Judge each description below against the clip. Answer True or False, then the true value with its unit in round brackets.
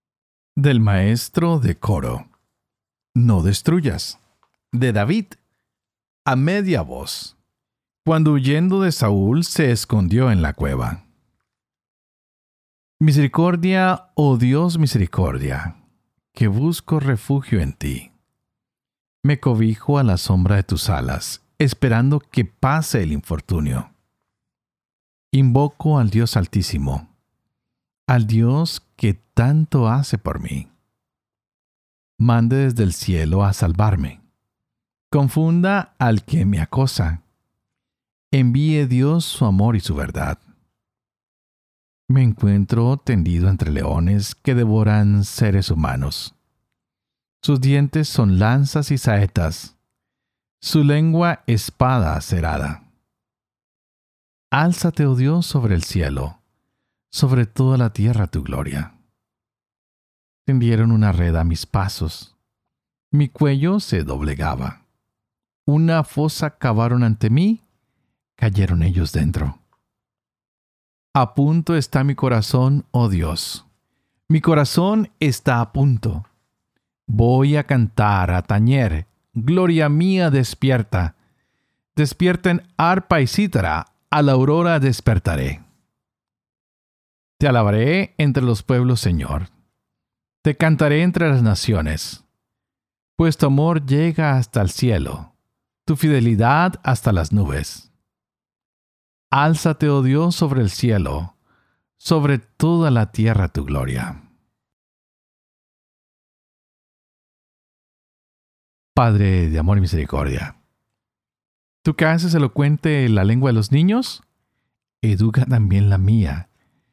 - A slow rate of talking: True (105 wpm)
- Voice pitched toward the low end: True (120 Hz)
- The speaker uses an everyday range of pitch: False (7.1 semitones)